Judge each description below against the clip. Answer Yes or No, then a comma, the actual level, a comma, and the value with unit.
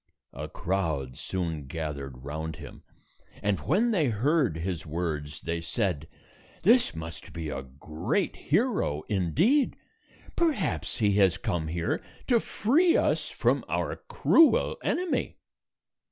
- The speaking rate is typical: No, slow, 125 wpm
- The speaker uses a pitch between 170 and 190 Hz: No, very low, 90 Hz